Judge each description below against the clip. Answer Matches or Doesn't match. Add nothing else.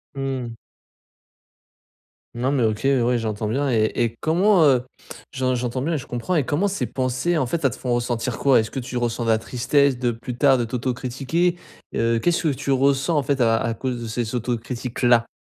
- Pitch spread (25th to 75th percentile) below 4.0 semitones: Matches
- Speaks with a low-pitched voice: Matches